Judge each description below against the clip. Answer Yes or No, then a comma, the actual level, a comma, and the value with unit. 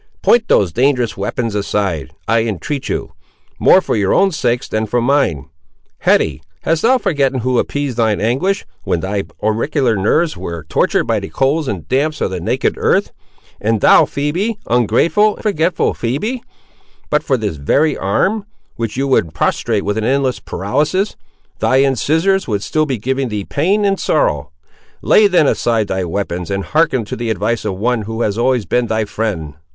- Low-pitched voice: Yes, low, 120 Hz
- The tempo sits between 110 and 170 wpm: No, average, 180 wpm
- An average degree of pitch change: No, wide, 6.4 semitones